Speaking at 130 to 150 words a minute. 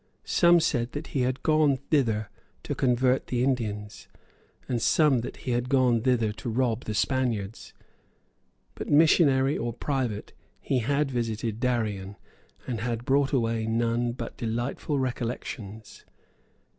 Yes: slow, 135 wpm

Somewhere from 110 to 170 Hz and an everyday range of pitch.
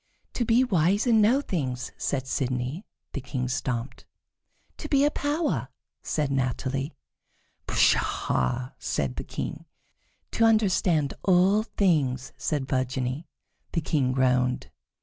No: medium, 140 Hz; wide, 7.9 semitones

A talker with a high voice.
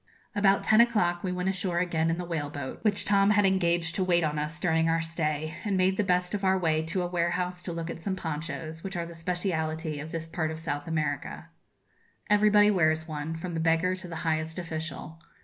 No: medium, 170 Hz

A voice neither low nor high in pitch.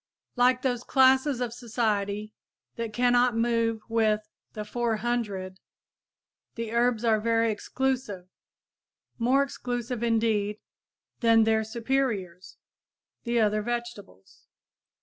No: high, 230 Hz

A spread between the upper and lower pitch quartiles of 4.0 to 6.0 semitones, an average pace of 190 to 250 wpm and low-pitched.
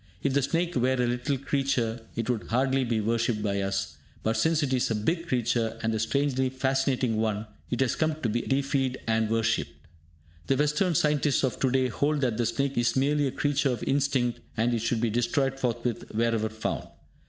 No: average, 3.4 semitones; average, 200 wpm; low, 125 Hz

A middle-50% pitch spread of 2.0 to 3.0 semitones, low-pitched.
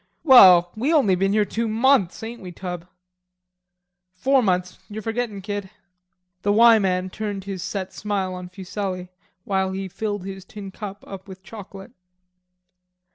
No: narrow, 2.6 semitones; high, 195 Hz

